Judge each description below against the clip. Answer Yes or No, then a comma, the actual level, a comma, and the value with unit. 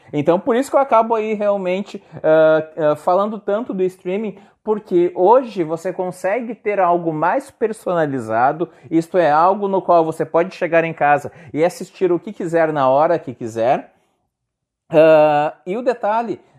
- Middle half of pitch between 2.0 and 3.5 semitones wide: No, average, 4.3 semitones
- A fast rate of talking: No, average, 165 wpm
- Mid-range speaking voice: Yes, medium, 175 Hz